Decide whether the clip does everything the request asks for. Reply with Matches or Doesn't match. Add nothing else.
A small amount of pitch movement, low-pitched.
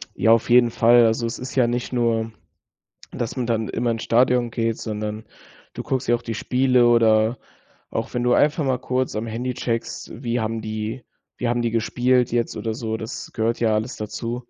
Matches